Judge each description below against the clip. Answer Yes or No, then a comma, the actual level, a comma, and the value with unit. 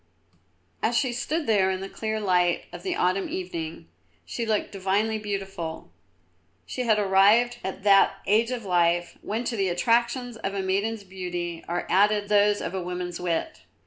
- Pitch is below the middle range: No, high, 195 Hz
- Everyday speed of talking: Yes, average, 170 wpm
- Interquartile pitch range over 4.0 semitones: No, average, 3.6 semitones